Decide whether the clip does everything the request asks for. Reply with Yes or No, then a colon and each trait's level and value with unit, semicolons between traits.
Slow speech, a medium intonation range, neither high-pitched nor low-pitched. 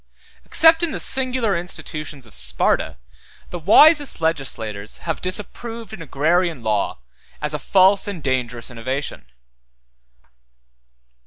No: slow, 110 wpm; wide, 8.1 semitones; medium, 165 Hz